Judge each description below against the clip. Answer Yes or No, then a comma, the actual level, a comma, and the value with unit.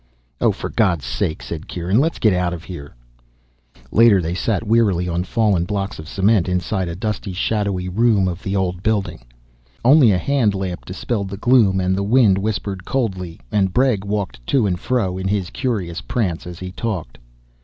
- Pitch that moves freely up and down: No, average, 3.4 semitones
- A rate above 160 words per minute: Yes, average, 185 wpm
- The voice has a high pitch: No, very low, 95 Hz